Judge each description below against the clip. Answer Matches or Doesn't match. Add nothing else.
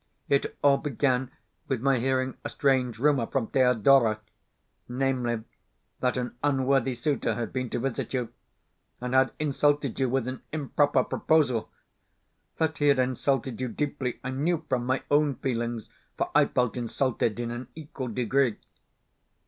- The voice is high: Doesn't match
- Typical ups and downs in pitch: Doesn't match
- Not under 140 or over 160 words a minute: Matches